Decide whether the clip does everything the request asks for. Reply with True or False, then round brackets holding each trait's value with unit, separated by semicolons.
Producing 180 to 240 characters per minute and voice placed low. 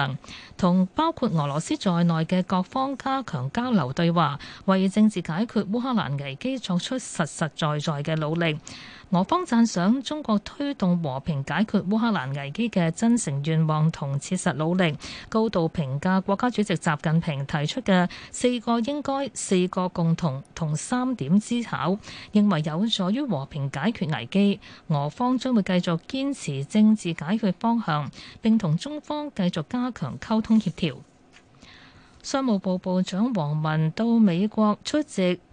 False (235 characters per minute; 185 Hz)